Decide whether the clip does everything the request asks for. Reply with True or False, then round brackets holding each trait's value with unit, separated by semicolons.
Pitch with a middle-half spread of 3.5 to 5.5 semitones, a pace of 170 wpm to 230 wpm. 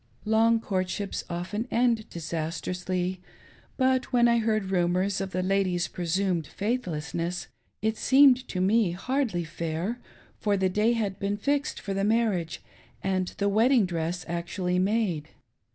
False (4.1 semitones; 135 wpm)